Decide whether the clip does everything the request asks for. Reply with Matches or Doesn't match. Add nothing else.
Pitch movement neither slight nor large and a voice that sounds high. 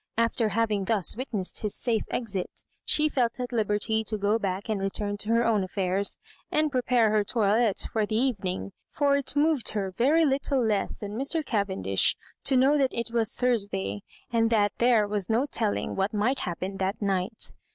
Matches